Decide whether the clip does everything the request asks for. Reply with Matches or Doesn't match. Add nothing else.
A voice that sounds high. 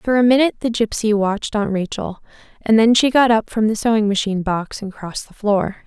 Matches